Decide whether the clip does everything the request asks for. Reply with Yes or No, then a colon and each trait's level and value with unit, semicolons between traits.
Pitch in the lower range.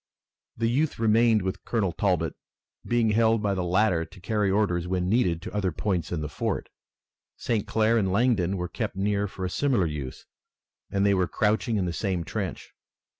Yes: low, 100 Hz